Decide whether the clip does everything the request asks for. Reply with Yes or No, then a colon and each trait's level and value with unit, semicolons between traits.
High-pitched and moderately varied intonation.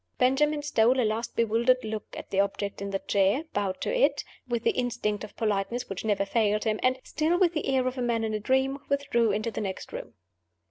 Yes: high, 230 Hz; average, 3.8 semitones